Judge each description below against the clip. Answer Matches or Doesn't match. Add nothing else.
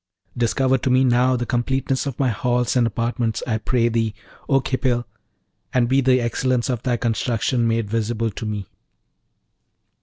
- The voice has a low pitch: Matches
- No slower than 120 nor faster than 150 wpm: Doesn't match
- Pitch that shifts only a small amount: Matches